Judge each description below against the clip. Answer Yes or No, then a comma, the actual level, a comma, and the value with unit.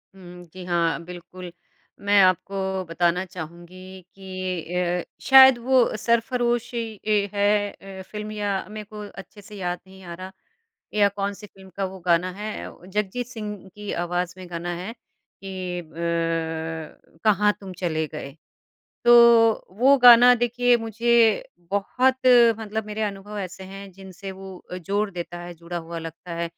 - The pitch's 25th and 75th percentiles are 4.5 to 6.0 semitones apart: No, average, 3.1 semitones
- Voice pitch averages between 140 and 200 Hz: Yes, high, 190 Hz